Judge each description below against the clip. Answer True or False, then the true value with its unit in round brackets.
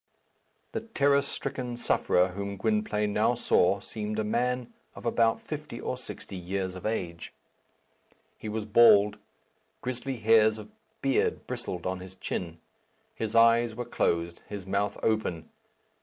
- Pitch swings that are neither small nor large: True (3.8 semitones)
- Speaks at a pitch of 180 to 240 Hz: False (110 Hz)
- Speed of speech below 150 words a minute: True (140 wpm)